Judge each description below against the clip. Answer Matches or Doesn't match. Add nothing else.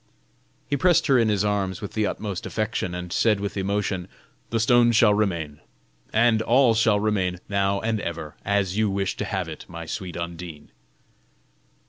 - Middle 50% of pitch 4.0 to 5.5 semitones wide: Doesn't match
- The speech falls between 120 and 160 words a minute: Doesn't match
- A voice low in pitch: Matches